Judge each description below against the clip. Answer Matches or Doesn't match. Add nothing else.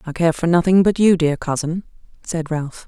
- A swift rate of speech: Matches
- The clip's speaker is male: Doesn't match